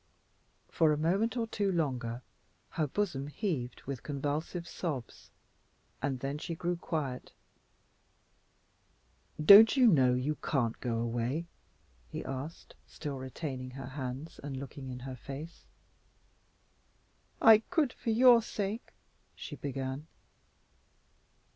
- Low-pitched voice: No, medium, 145 Hz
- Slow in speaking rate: Yes, slow, 115 wpm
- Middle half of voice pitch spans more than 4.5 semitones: Yes, average, 5.1 semitones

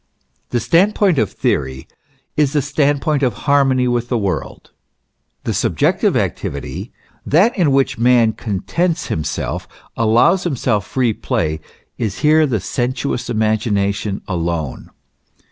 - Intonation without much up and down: No, wide, 5.5 semitones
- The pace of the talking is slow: Yes, slow, 130 wpm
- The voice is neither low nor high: No, low, 125 Hz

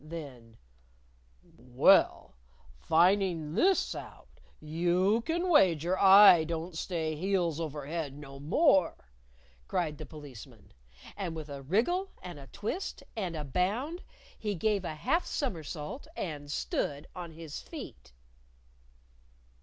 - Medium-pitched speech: Yes, medium, 165 Hz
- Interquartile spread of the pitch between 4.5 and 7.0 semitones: Yes, average, 4.8 semitones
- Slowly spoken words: Yes, slow, 120 wpm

